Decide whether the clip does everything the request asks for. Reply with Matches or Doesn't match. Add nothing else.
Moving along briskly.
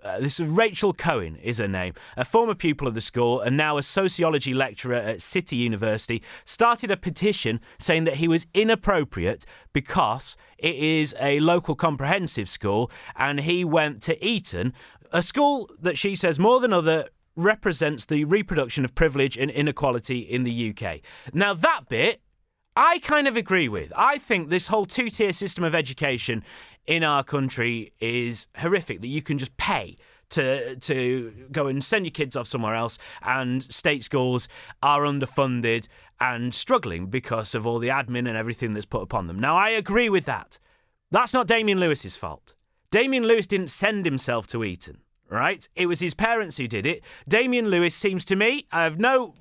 Doesn't match